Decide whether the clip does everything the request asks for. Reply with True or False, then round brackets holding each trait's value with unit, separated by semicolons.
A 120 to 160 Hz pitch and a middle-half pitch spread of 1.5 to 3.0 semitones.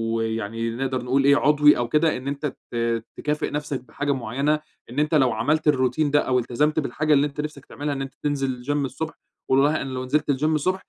True (140 Hz; 2.7 semitones)